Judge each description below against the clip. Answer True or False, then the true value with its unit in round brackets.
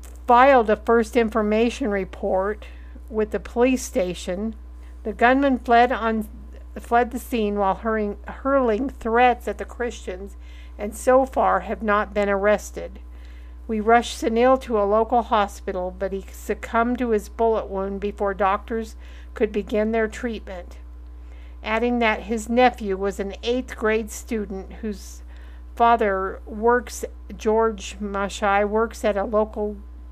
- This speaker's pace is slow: True (130 wpm)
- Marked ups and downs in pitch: False (3.4 semitones)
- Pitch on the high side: True (210 Hz)